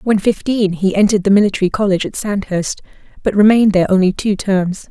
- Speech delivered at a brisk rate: No, average, 185 wpm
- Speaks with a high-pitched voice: Yes, high, 200 Hz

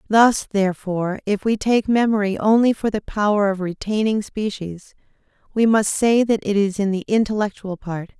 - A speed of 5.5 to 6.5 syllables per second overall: No, 5.0 syllables/s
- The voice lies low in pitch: No, high, 205 Hz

